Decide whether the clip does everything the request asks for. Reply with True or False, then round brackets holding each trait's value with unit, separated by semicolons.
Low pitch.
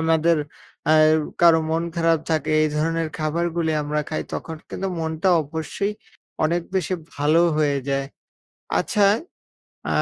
False (160 Hz)